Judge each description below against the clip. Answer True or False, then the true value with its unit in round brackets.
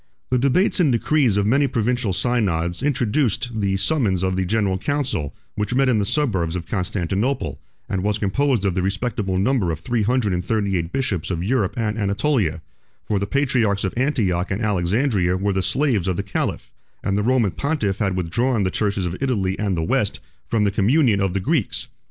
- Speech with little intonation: False (5.0 semitones)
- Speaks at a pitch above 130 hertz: False (105 Hz)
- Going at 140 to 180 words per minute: False (195 wpm)